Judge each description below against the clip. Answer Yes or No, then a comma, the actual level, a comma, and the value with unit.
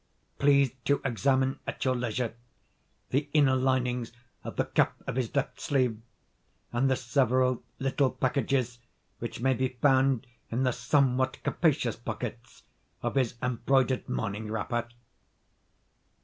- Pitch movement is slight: Yes, narrow, 2.0 semitones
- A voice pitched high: No, low, 130 Hz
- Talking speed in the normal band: No, slow, 130 wpm